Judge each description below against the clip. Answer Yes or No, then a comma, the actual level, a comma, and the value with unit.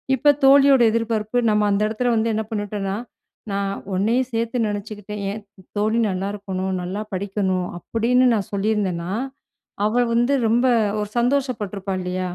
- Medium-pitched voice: No, high, 210 Hz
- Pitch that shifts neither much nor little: Yes, average, 3.0 semitones